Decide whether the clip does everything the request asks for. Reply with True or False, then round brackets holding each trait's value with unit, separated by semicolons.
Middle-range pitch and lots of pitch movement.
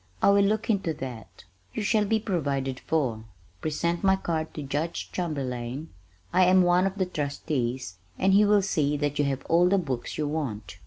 True (155 Hz; 5.7 semitones)